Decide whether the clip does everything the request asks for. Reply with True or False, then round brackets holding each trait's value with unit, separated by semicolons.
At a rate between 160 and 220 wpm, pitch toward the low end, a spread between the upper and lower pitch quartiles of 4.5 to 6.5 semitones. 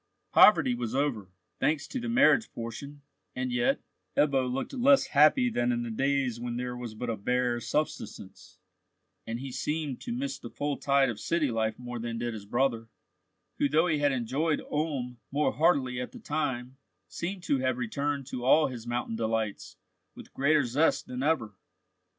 False (180 wpm; 130 Hz; 3.9 semitones)